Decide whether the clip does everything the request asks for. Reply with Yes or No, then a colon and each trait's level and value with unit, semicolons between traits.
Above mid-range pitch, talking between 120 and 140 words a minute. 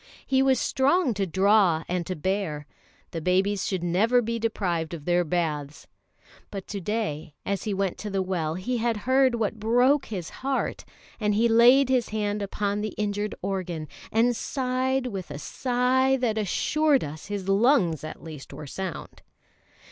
No: high, 205 Hz; average, 170 wpm